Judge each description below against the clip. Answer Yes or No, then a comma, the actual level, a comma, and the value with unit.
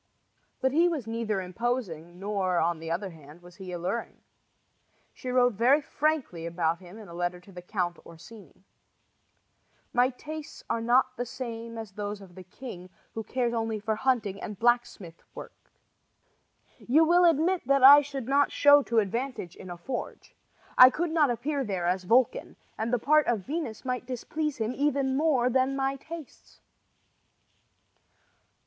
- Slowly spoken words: No, average, 165 wpm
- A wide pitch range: Yes, wide, 6.2 semitones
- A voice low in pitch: No, high, 235 Hz